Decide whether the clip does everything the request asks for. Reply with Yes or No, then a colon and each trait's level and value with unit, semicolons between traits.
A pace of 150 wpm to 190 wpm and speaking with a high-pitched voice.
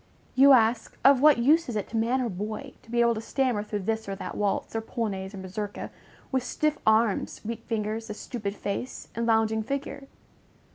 No: average, 200 wpm; high, 225 Hz